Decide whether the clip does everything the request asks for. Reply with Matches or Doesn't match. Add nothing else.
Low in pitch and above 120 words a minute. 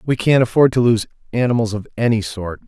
Matches